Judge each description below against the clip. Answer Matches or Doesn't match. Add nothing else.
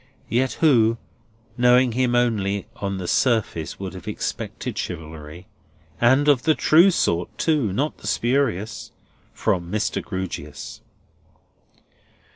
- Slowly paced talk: Matches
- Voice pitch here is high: Doesn't match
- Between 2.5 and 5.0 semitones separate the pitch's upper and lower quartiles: Doesn't match